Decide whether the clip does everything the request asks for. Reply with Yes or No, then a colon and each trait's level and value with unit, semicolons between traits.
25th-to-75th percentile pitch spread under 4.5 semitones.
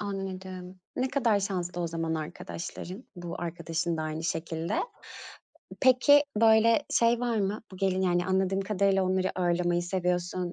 Yes: narrow, 2.6 semitones